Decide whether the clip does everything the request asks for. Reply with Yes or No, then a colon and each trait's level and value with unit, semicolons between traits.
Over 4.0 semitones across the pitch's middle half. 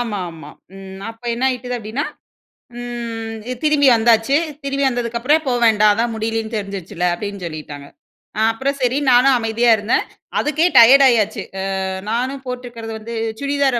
No: average, 3.1 semitones